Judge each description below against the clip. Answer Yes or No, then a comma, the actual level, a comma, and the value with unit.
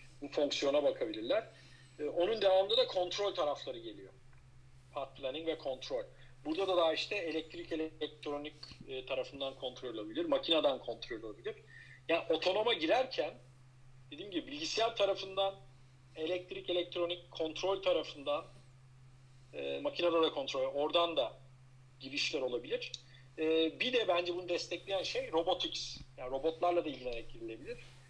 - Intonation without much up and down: No, wide, 5.5 semitones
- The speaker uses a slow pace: No, average, 115 wpm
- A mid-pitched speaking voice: Yes, medium, 150 Hz